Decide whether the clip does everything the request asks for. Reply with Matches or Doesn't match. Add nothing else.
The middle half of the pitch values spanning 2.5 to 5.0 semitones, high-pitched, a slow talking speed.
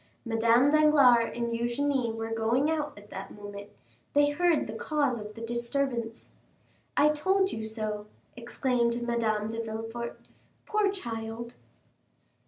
Matches